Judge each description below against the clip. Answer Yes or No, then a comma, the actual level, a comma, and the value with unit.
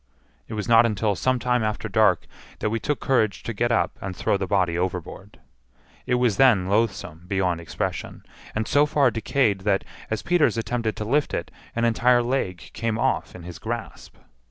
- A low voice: Yes, low, 110 Hz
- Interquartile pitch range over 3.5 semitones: Yes, average, 3.9 semitones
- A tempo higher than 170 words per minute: Yes, average, 185 wpm